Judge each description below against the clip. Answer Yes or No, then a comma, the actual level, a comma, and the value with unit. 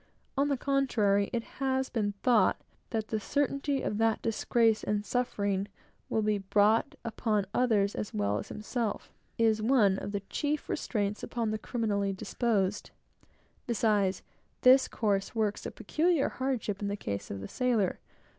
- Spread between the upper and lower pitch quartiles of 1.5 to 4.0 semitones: Yes, average, 3.5 semitones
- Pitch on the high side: Yes, high, 215 Hz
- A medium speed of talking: Yes, average, 150 wpm